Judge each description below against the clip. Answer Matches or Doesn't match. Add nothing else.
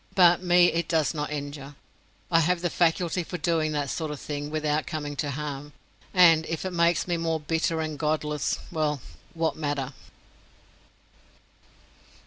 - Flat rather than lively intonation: Matches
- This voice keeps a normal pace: Matches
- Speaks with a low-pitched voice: Doesn't match